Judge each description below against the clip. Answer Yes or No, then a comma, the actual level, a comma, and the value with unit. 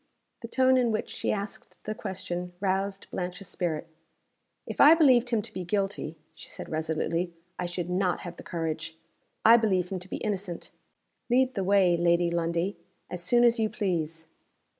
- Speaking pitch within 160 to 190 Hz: Yes, medium, 185 Hz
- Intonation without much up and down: No, average, 3.9 semitones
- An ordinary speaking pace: Yes, average, 175 wpm